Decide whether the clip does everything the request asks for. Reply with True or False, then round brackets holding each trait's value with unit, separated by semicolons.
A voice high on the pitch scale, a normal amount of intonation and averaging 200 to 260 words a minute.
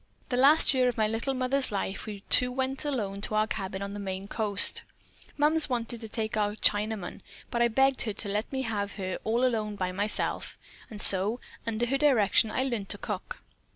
True (220 Hz; 3.8 semitones; 205 wpm)